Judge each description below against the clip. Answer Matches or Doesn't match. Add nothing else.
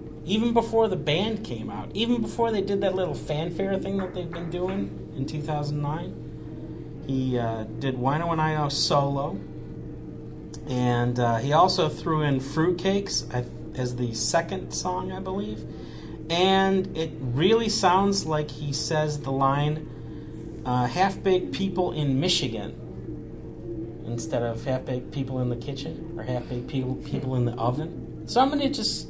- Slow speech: Doesn't match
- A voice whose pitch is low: Doesn't match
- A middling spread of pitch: Doesn't match